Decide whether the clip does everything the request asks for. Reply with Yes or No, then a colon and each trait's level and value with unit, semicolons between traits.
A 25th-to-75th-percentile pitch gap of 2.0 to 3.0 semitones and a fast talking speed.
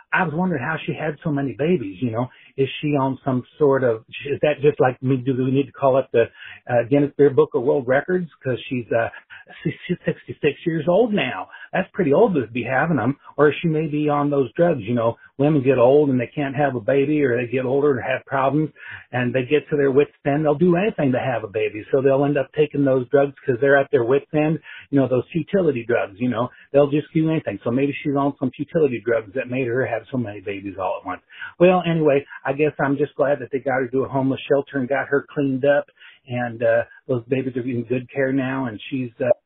Yes: narrow, 2.5 semitones; fast, 245 wpm